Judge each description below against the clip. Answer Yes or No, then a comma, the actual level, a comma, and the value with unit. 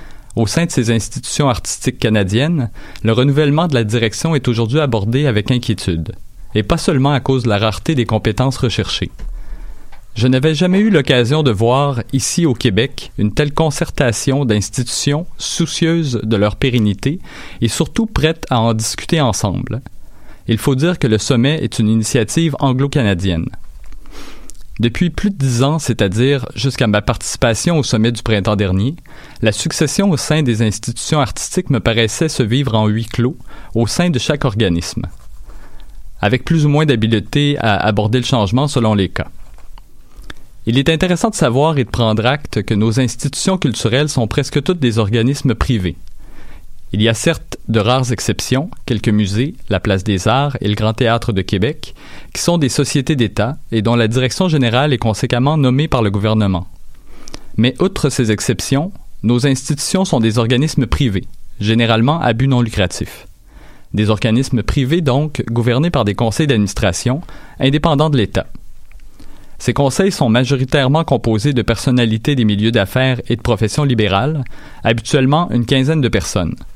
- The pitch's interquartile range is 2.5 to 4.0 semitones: No, average, 4.7 semitones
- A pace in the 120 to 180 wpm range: Yes, average, 165 wpm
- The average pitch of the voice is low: Yes, low, 125 Hz